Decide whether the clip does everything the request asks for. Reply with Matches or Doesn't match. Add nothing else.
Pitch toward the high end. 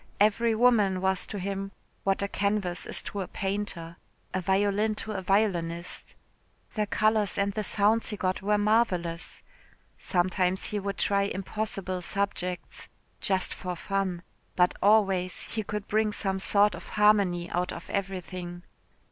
Matches